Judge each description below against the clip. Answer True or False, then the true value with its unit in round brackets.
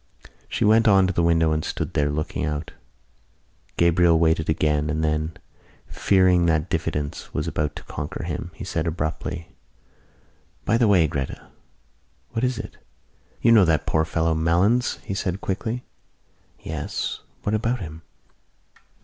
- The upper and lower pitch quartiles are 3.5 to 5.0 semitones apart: True (3.9 semitones)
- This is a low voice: True (85 Hz)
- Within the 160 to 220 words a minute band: False (150 wpm)